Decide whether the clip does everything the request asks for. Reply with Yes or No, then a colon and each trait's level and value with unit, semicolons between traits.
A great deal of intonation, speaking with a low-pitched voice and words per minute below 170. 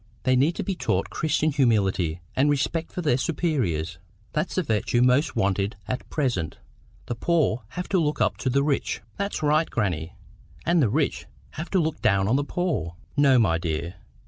No: wide, 7.8 semitones; low, 130 Hz; average, 185 wpm